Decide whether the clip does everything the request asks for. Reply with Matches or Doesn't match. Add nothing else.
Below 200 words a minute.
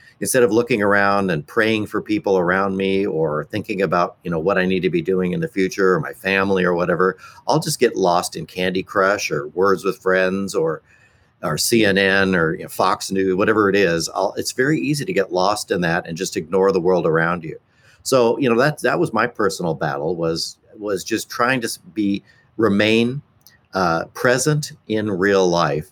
Doesn't match